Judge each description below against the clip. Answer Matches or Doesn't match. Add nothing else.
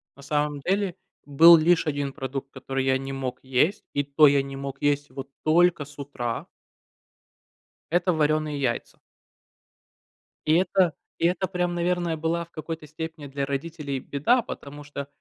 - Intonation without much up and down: Doesn't match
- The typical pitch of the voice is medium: Matches